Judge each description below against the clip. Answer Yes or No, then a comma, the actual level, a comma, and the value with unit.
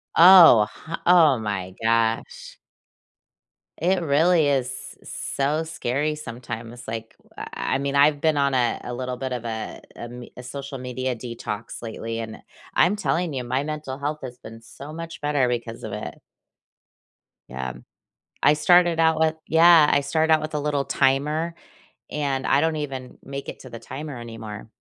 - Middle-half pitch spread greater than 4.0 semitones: Yes, average, 4.5 semitones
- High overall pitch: No, medium, 140 Hz